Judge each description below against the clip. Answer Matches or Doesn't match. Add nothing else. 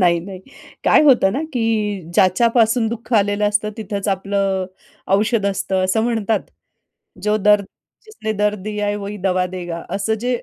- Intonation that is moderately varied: Doesn't match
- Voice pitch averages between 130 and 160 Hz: Doesn't match